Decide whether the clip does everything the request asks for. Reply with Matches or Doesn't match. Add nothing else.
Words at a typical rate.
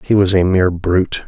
Doesn't match